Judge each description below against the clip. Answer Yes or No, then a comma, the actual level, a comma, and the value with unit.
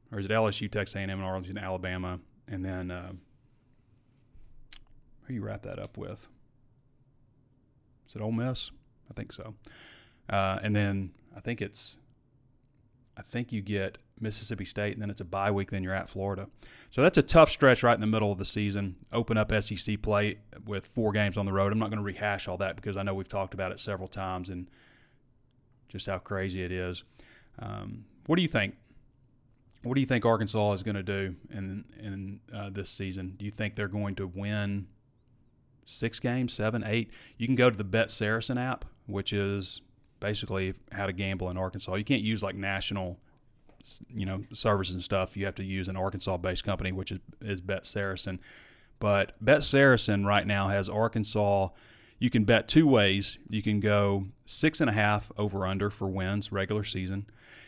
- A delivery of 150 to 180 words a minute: No, average, 195 wpm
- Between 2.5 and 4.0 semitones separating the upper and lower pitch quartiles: Yes, average, 3.4 semitones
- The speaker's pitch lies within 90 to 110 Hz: Yes, low, 105 Hz